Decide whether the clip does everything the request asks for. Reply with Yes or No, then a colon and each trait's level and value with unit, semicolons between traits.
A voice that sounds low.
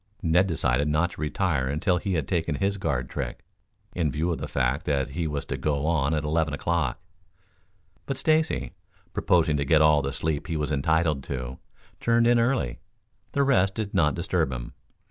Yes: very low, 80 Hz